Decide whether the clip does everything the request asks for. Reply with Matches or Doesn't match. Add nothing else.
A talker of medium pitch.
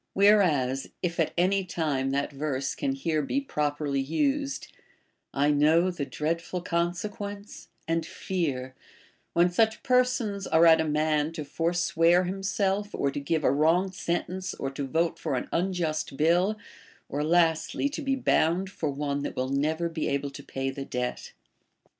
Matches